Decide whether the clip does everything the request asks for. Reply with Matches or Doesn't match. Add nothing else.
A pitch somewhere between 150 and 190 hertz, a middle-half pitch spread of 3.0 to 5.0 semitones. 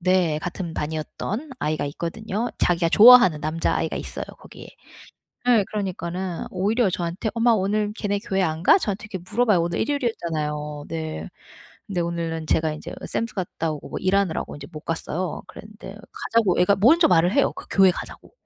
Matches